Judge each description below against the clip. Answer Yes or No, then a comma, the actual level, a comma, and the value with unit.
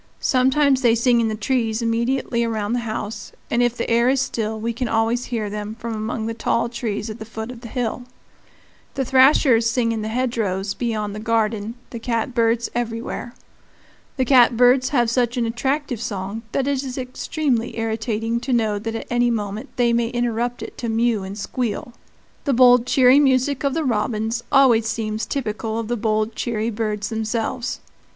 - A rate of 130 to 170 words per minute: No, average, 185 wpm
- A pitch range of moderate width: No, narrow, 2.1 semitones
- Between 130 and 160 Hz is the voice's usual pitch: No, high, 235 Hz